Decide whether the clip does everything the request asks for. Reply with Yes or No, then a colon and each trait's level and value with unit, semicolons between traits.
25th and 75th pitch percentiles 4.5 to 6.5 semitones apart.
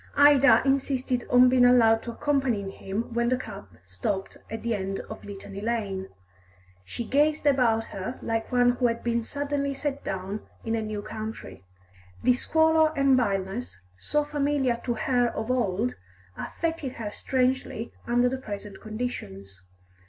No: average, 4.1 semitones